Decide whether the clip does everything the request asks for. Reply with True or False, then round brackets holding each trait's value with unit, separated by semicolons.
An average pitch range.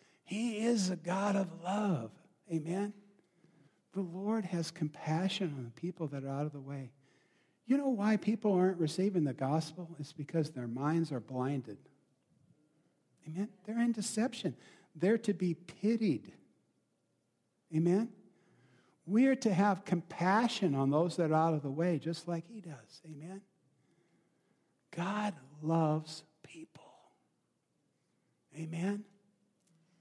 True (4.5 semitones)